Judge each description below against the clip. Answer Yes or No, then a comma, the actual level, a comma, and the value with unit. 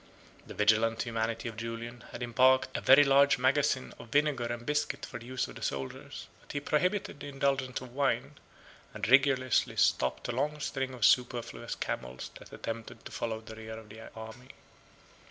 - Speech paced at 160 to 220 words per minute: Yes, average, 180 wpm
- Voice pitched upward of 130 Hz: No, low, 120 Hz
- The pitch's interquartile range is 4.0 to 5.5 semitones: No, average, 3.3 semitones